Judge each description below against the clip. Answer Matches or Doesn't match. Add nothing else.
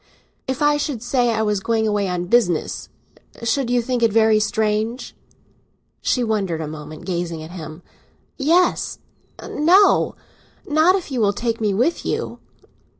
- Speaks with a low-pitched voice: Doesn't match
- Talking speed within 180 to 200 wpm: Doesn't match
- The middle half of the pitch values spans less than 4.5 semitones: Doesn't match